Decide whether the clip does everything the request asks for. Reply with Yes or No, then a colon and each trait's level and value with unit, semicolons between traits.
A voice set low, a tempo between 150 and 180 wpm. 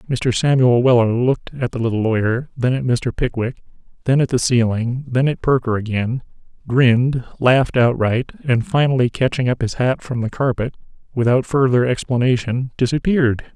Yes: low, 125 Hz; average, 160 wpm